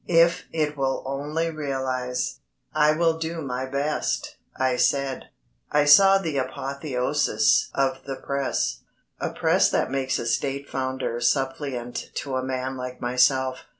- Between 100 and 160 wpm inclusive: Yes, average, 140 wpm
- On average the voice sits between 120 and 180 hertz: Yes, low, 135 Hz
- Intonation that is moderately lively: No, narrow, 2.3 semitones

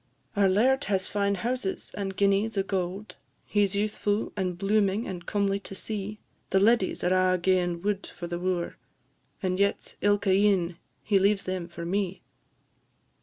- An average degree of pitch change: No, narrow, 1.8 semitones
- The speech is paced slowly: No, average, 170 wpm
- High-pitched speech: Yes, high, 195 Hz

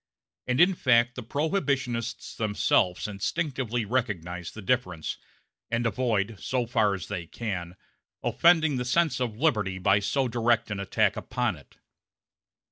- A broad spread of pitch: No, average, 4.4 semitones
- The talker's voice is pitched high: No, low, 115 Hz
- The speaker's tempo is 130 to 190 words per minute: Yes, slow, 135 wpm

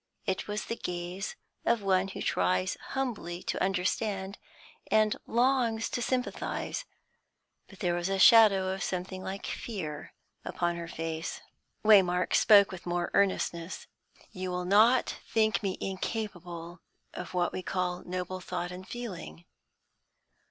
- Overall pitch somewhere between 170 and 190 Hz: Yes, medium, 185 Hz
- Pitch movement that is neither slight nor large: Yes, average, 3.1 semitones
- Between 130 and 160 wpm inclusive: Yes, slow, 135 wpm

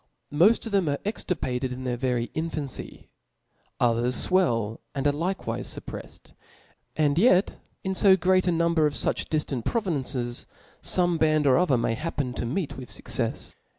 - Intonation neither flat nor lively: No, wide, 6.0 semitones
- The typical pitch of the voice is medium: Yes, medium, 150 Hz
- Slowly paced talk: No, average, 165 wpm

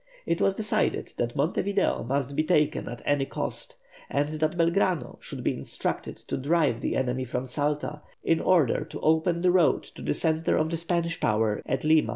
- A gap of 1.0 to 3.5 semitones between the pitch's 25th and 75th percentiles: No, average, 4.2 semitones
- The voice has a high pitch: No, medium, 155 Hz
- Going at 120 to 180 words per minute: No, average, 190 wpm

